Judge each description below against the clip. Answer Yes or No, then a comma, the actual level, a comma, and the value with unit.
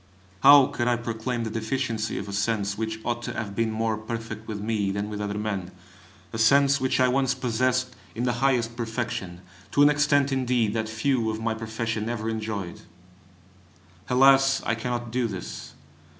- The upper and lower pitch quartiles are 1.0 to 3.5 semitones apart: Yes, narrow, 2.6 semitones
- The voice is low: Yes, low, 115 Hz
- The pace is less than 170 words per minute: No, average, 180 wpm